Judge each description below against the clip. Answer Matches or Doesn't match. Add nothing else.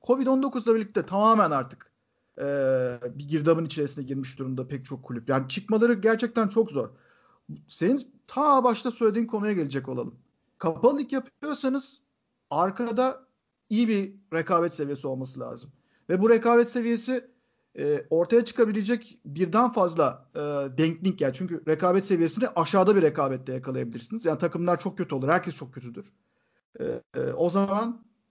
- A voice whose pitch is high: Matches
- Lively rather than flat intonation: Matches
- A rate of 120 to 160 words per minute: Matches